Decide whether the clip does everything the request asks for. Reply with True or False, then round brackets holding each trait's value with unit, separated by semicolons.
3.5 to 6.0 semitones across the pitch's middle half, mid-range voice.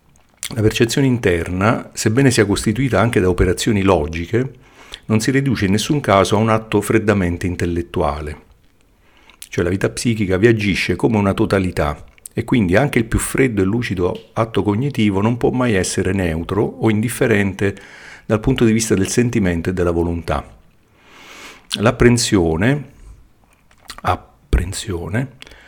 False (4.6 semitones; 105 Hz)